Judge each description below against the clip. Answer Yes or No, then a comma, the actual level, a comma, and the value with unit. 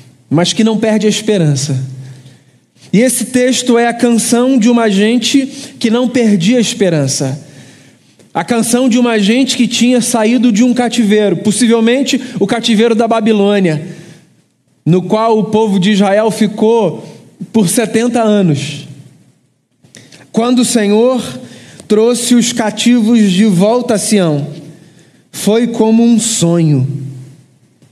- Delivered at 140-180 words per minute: No, average, 130 wpm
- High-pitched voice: Yes, high, 215 Hz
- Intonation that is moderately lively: No, wide, 6.7 semitones